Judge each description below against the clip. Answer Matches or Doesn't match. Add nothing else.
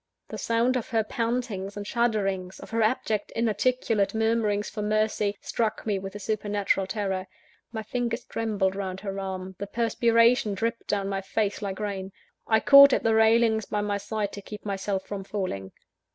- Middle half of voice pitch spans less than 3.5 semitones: Matches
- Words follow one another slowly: Doesn't match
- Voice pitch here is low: Doesn't match